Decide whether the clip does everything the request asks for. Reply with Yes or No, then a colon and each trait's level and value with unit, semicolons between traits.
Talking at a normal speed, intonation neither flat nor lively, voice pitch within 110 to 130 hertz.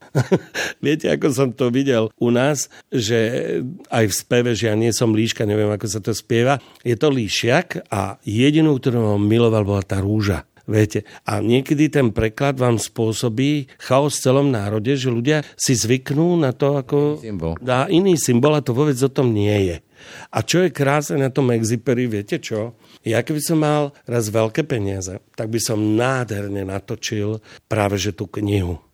No: fast, 175 wpm; average, 4.6 semitones; low, 120 Hz